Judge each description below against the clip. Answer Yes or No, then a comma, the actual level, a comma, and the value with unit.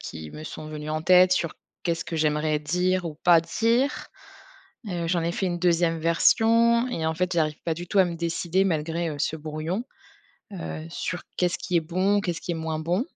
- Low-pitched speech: No, medium, 170 Hz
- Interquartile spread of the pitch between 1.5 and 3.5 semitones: Yes, narrow, 2.5 semitones